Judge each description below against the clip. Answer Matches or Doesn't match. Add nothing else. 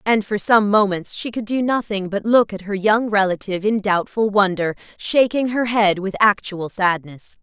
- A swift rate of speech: Doesn't match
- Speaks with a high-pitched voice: Matches